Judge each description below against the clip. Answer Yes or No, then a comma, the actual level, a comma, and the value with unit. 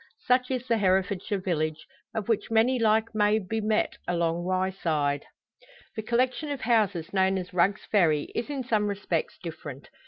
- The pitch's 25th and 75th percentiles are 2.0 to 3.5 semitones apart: No, average, 4.0 semitones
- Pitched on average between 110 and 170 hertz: No, high, 205 Hz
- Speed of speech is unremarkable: Yes, average, 160 wpm